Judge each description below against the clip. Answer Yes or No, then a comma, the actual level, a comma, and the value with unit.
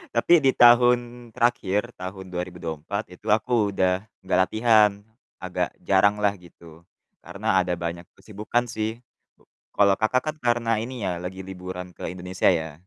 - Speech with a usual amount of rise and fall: Yes, average, 4.3 semitones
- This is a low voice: Yes, low, 100 Hz